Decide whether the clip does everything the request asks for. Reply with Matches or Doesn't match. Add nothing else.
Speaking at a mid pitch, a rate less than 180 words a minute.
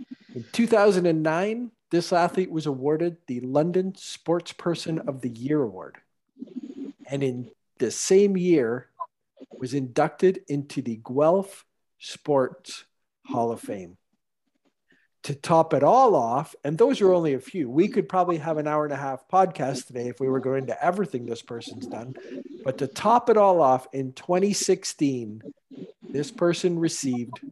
Matches